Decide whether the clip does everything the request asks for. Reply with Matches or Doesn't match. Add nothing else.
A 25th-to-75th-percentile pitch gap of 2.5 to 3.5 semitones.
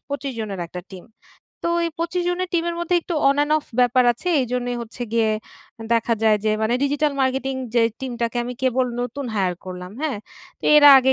Doesn't match